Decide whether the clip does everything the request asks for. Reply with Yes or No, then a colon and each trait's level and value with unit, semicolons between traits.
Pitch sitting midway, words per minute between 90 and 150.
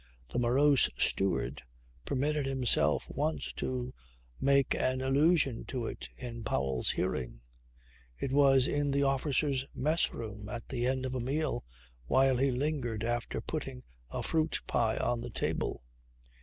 No: low, 130 Hz; average, 145 wpm